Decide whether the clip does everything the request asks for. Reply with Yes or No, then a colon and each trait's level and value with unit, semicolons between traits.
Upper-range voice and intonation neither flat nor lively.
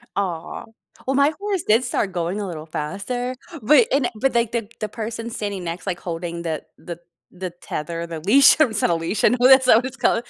No: high, 205 Hz; wide, 6.4 semitones